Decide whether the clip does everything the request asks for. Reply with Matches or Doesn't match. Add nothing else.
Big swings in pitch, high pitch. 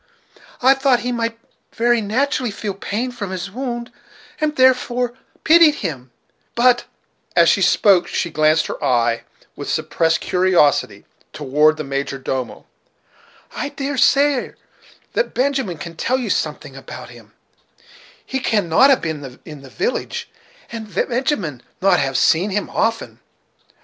Matches